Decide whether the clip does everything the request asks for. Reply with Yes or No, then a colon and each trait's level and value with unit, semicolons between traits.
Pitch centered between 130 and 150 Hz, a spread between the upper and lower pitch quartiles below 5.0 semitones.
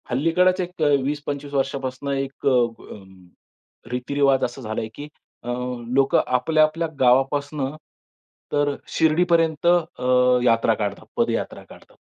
Yes: medium, 140 Hz; average, 3.5 semitones